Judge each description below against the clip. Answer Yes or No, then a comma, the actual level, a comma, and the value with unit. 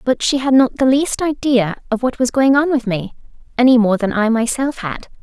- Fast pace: Yes, fast, 230 wpm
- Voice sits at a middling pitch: No, very high, 250 Hz